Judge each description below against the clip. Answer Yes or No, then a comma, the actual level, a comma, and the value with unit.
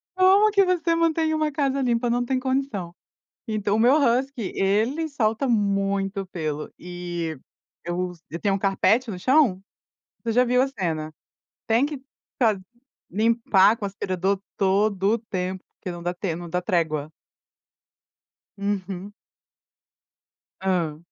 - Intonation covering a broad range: Yes, wide, 5.8 semitones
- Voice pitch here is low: No, high, 205 Hz